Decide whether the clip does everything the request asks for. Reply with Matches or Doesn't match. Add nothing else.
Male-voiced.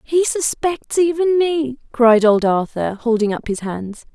Doesn't match